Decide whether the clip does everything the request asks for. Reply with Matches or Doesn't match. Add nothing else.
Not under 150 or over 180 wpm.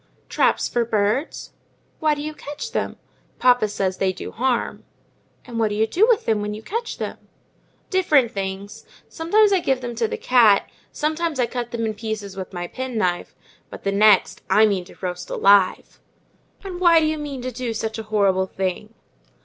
Doesn't match